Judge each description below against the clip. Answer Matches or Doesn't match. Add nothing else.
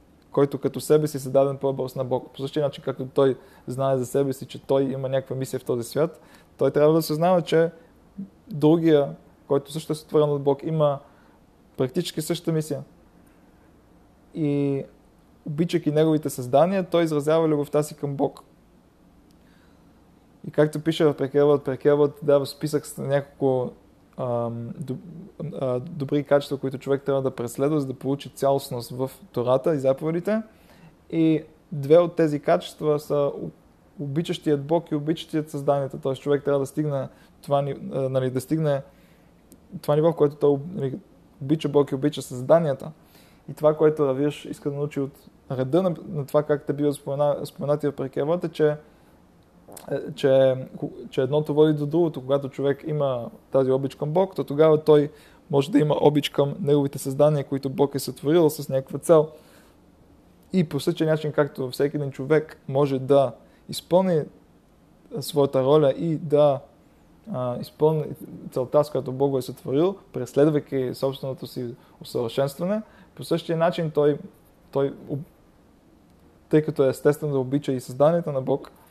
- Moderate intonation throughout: Doesn't match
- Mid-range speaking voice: Matches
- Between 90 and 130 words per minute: Doesn't match